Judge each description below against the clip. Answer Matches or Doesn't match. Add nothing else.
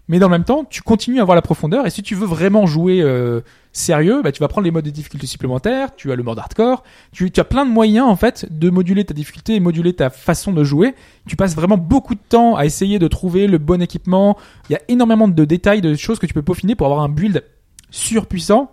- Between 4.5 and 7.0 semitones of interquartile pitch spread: Matches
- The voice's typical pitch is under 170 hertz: Doesn't match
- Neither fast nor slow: Doesn't match